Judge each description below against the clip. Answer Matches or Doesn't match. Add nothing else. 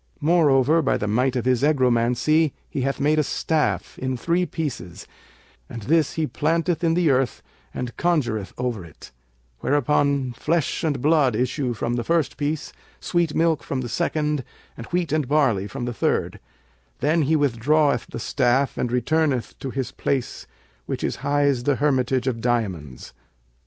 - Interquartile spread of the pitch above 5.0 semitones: Doesn't match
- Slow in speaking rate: Doesn't match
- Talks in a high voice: Doesn't match